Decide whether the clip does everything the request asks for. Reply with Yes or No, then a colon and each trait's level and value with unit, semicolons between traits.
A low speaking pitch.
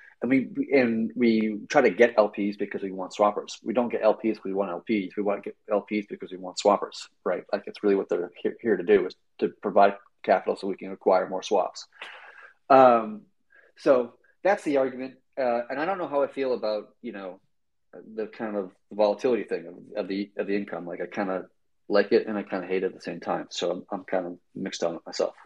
Yes: low, 105 Hz